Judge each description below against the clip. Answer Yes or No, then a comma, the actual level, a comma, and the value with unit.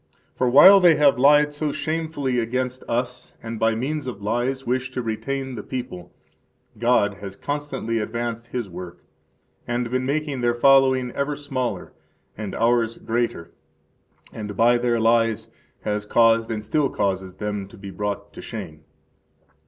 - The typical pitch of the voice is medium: No, low, 120 Hz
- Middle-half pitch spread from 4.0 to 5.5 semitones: No, average, 3.6 semitones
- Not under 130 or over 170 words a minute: Yes, average, 155 wpm